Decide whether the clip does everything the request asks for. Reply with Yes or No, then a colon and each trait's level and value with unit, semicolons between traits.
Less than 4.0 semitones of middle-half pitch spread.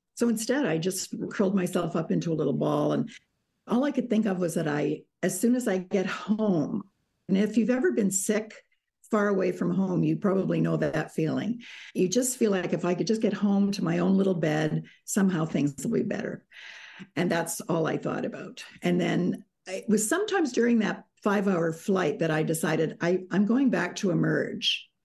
Yes: average, 3.6 semitones